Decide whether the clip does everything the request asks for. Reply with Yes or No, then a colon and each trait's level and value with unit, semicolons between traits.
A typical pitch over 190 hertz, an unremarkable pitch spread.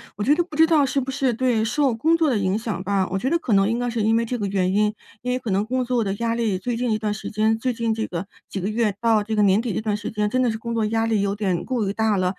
Yes: high, 220 Hz; average, 3.1 semitones